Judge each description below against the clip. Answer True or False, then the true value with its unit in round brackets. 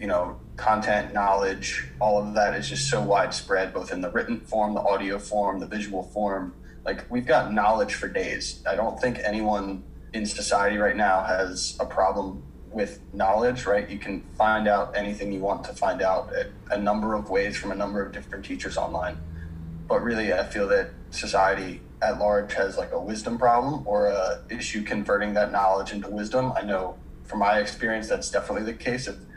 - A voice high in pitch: False (100 Hz)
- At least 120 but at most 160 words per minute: False (190 wpm)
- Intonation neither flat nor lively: False (2.0 semitones)